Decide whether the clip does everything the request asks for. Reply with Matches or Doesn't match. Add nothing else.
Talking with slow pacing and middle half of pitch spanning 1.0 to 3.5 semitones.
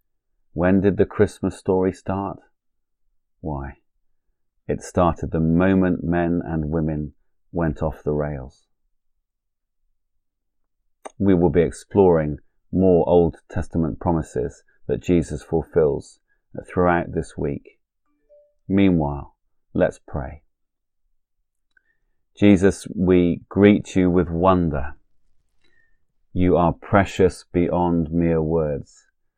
Matches